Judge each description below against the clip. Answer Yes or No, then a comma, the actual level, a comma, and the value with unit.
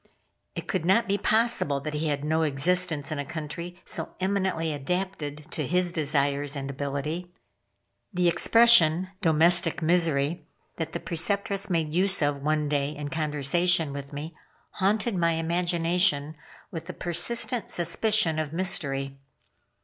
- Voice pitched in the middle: Yes, medium, 165 Hz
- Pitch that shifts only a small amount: No, average, 3.6 semitones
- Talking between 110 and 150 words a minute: Yes, average, 140 wpm